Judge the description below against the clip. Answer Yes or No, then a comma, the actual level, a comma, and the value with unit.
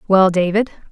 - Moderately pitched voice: No, high, 195 Hz